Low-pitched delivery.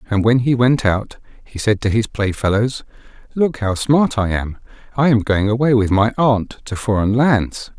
Yes: low, 115 Hz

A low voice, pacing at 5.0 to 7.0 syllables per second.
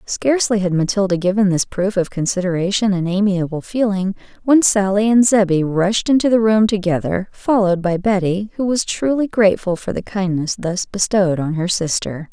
No: high, 195 Hz; 5.3 syllables/s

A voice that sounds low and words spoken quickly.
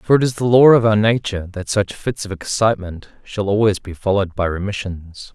Yes: low, 100 Hz; fast, 215 wpm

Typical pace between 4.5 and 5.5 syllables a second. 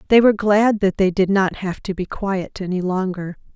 Yes: 5.0 syllables/s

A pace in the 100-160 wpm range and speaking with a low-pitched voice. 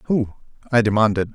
Yes: slow, 135 wpm; low, 110 Hz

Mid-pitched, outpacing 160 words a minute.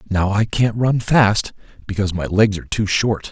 No: low, 105 Hz; average, 200 wpm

